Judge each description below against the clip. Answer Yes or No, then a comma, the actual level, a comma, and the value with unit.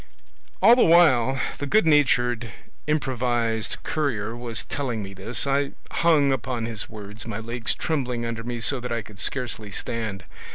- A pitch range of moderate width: Yes, average, 3.6 semitones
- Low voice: Yes, low, 120 Hz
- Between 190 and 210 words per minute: No, average, 160 wpm